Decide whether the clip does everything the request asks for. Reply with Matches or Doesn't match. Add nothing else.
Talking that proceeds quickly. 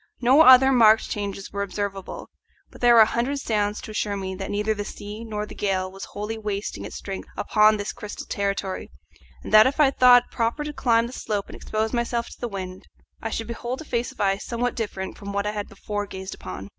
Matches